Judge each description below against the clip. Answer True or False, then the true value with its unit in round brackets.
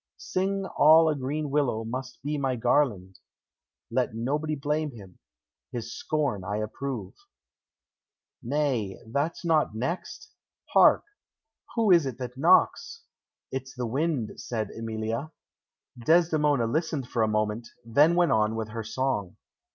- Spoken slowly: True (130 wpm)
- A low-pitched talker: True (130 Hz)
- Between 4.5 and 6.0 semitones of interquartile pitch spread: True (5.4 semitones)